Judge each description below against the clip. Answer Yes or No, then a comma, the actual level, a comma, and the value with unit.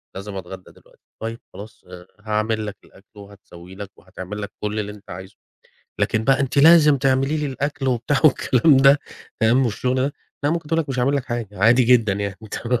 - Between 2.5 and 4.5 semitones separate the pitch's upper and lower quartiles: No, average, 4.9 semitones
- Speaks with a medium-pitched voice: No, low, 115 Hz